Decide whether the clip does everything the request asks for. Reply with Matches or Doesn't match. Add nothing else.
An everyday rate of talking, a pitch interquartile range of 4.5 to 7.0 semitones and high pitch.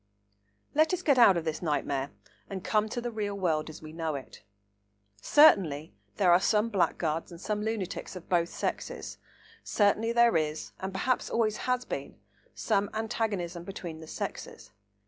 Matches